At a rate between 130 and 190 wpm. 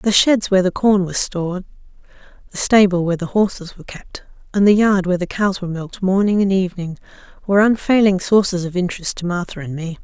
No: fast, 205 wpm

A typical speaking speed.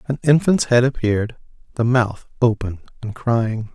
Yes: average, 145 wpm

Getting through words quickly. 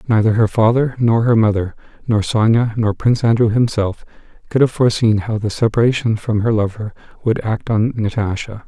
No: average, 175 wpm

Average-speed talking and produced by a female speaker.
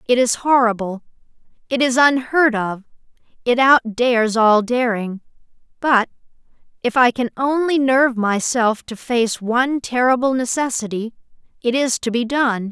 No: slow, 130 wpm; female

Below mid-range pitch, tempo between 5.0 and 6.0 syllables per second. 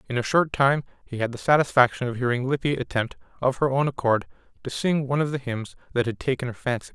No: low, 130 Hz; 6.4 syllables/s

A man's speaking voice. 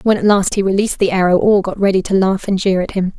No: female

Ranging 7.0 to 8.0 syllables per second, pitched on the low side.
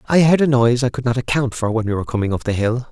Yes: 7.3 syllables/s; low, 120 Hz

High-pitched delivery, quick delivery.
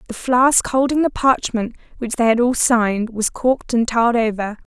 No: high, 235 Hz; average, 190 wpm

